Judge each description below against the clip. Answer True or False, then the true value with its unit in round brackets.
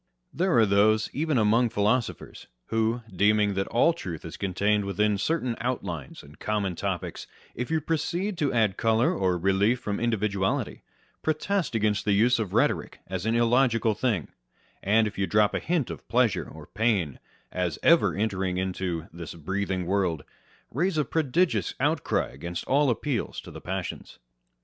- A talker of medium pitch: False (105 Hz)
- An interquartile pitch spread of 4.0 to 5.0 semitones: True (4.4 semitones)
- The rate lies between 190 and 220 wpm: False (165 wpm)